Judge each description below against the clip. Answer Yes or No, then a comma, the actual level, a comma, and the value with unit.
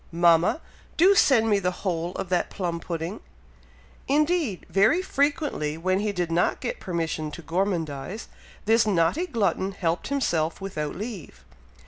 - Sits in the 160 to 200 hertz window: Yes, medium, 185 Hz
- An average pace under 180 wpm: Yes, average, 140 wpm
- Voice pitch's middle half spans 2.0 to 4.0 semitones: No, average, 5.3 semitones